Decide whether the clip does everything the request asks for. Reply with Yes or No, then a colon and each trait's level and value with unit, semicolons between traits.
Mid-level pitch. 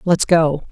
Yes: medium, 160 Hz